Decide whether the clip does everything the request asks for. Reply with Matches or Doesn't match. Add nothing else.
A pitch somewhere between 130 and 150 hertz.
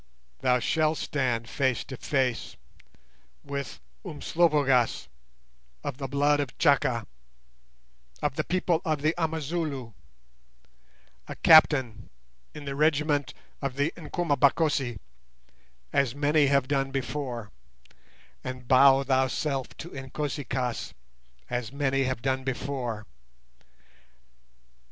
Matches